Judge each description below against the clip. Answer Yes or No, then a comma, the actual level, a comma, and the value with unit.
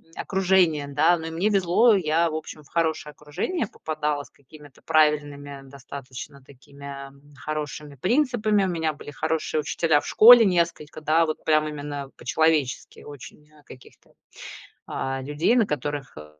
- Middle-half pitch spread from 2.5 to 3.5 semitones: Yes, average, 2.9 semitones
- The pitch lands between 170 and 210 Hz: No, medium, 155 Hz